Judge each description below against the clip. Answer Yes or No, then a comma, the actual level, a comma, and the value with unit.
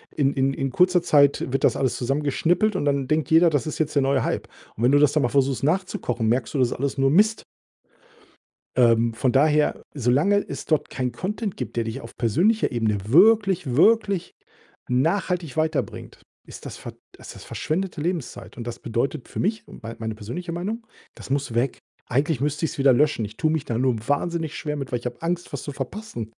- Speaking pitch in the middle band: Yes, medium, 145 Hz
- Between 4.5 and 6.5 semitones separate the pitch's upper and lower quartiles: Yes, average, 5.1 semitones